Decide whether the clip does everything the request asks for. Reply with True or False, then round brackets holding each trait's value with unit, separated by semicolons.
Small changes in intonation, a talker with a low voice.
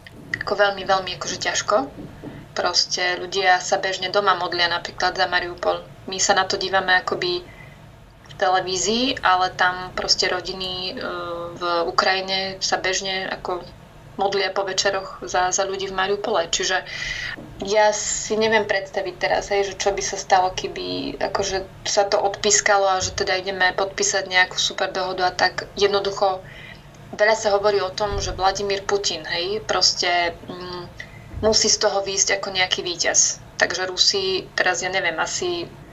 False (1.8 semitones; 190 Hz)